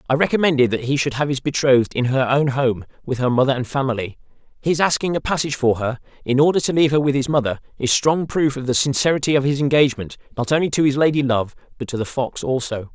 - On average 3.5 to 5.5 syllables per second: No, 6.6 syllables/s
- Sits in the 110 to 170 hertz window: Yes, low, 135 Hz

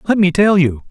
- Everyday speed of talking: No, fast, 265 wpm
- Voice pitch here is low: No, medium, 175 Hz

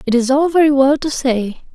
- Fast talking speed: Yes, fast, 240 wpm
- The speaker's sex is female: Yes, female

